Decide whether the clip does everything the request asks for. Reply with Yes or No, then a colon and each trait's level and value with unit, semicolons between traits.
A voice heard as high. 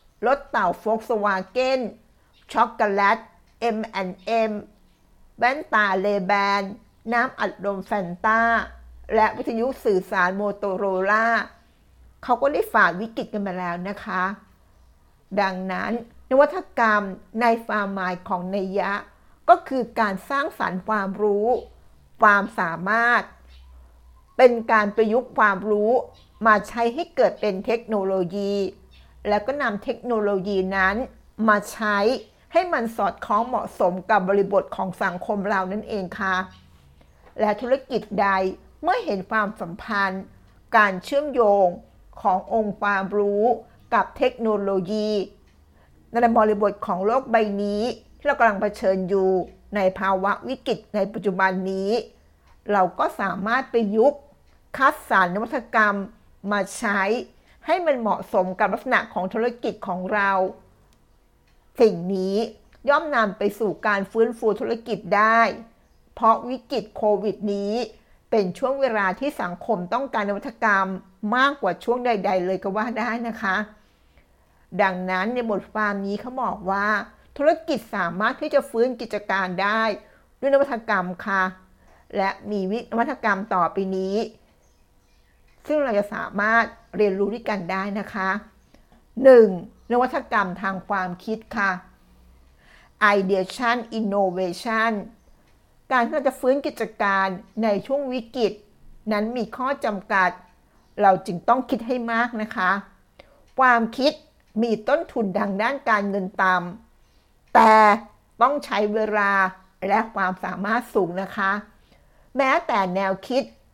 Yes: high, 210 Hz